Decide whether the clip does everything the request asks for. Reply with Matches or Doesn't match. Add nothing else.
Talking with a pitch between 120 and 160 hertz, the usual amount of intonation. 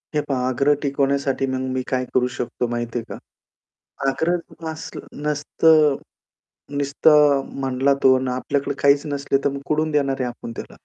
Doesn't match